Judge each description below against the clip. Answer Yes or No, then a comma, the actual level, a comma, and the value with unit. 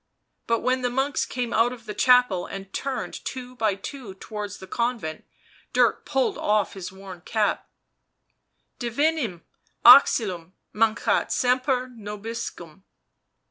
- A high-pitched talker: Yes, high, 230 Hz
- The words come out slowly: Yes, slow, 130 wpm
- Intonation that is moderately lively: Yes, average, 4.3 semitones